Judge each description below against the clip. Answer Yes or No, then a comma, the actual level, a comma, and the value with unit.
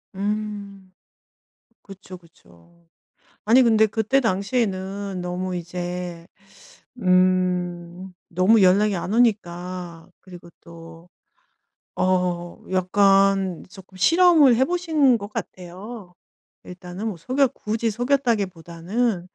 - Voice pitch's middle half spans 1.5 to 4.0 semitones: Yes, average, 3.6 semitones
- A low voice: No, high, 190 Hz